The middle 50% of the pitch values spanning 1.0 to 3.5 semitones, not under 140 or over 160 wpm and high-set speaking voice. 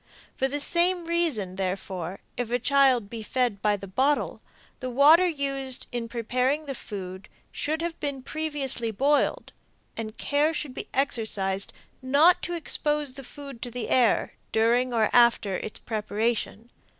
No: average, 4.7 semitones; average, 150 wpm; very high, 255 Hz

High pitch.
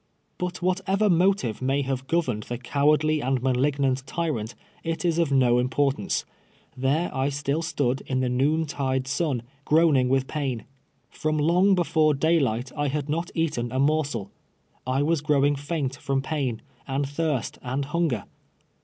No: medium, 140 Hz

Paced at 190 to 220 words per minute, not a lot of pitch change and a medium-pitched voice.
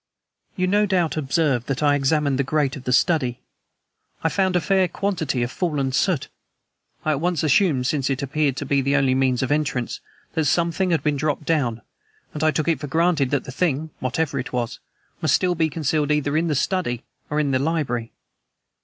No: fast, 205 wpm; average, 3.4 semitones; medium, 150 Hz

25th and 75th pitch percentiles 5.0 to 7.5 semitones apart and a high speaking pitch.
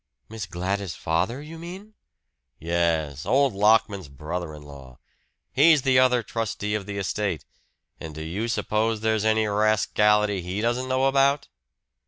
No: wide, 5.6 semitones; low, 105 Hz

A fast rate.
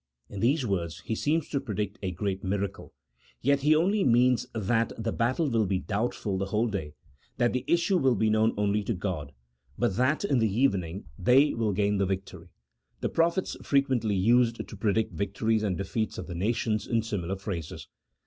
No: average, 195 wpm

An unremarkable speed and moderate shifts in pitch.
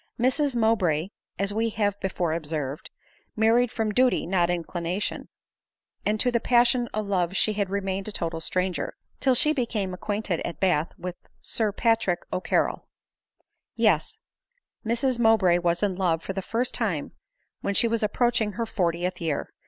Yes: average, 160 wpm; average, 4.4 semitones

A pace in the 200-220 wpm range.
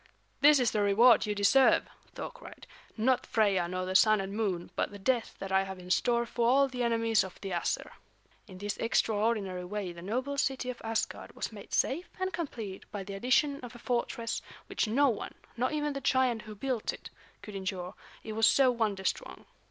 Yes: fast, 205 wpm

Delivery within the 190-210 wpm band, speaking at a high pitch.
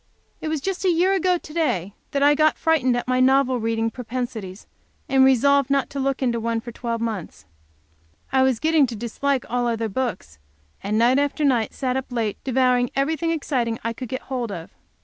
Yes: average, 200 wpm; very high, 255 Hz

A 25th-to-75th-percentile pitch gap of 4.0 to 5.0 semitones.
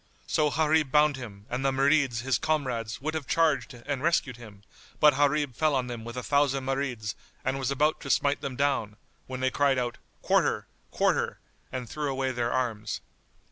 No: average, 2.8 semitones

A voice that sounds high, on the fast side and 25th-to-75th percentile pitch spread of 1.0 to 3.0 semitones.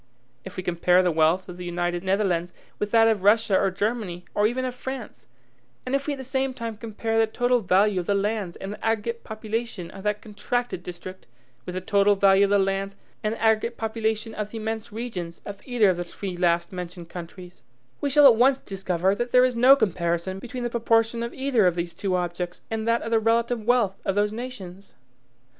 No: high, 210 Hz; fast, 215 wpm; average, 4.0 semitones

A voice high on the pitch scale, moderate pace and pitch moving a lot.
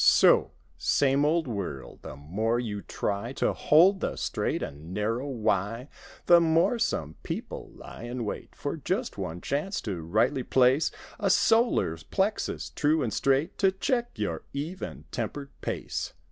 No: low, 135 Hz; average, 150 wpm; wide, 8.3 semitones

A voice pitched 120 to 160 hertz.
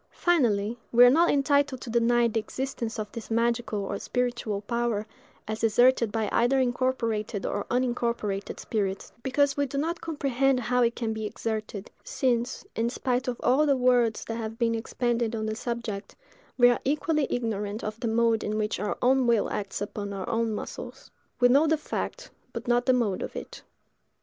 No: high, 235 Hz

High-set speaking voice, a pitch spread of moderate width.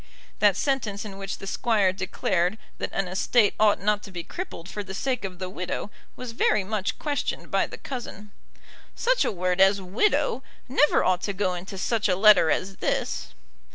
Yes: high, 200 Hz; average, 3.2 semitones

